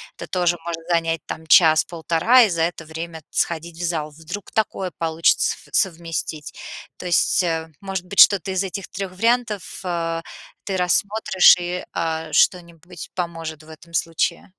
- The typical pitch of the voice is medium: Yes, medium, 170 Hz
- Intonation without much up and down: Yes, narrow, 2.3 semitones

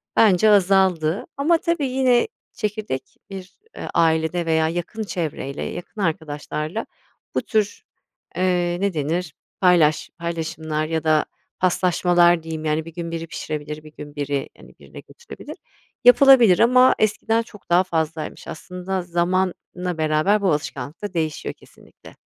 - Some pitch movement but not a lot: Yes, average, 3.8 semitones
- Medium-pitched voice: Yes, medium, 175 Hz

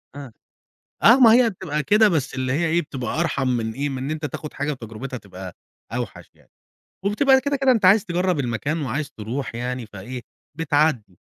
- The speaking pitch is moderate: Yes, medium, 145 Hz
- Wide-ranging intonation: Yes, wide, 6.5 semitones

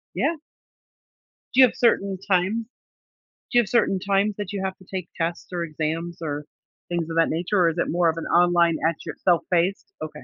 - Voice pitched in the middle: Yes, medium, 175 Hz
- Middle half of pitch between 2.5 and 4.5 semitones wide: Yes, average, 2.9 semitones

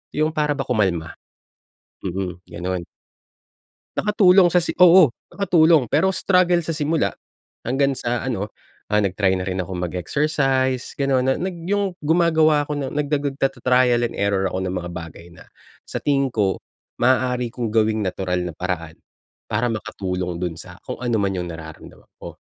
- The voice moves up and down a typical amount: No, wide, 8.2 semitones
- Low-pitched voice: Yes, low, 125 Hz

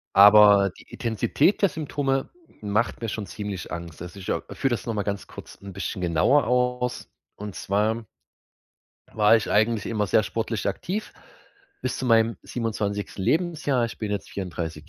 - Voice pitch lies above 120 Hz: No, low, 110 Hz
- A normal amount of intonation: Yes, average, 3.7 semitones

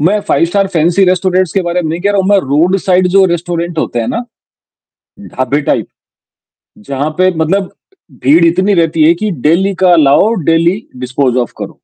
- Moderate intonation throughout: Yes, average, 3.3 semitones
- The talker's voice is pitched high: No, medium, 175 Hz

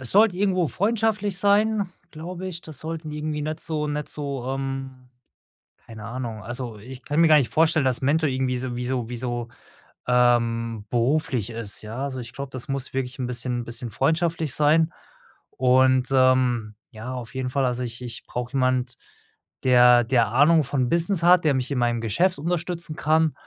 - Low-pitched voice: Yes, low, 130 Hz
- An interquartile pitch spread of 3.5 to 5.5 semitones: Yes, average, 4.3 semitones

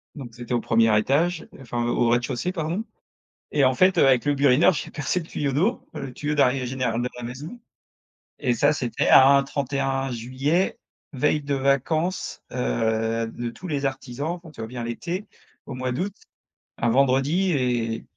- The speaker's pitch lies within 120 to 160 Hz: Yes, low, 135 Hz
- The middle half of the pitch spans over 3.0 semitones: Yes, average, 3.7 semitones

